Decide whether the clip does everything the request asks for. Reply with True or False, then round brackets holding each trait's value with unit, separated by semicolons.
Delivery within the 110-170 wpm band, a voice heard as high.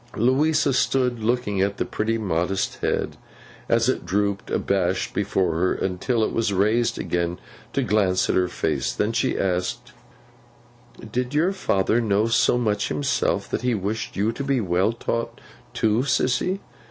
False (155 wpm; 110 Hz)